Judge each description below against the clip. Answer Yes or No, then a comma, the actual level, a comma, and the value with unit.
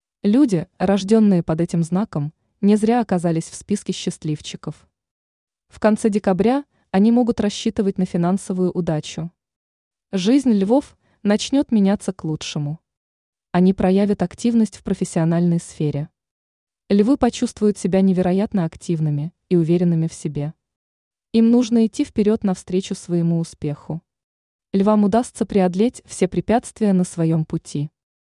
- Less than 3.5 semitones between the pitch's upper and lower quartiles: No, average, 4.3 semitones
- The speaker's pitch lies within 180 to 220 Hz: Yes, high, 190 Hz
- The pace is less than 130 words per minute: Yes, average, 120 wpm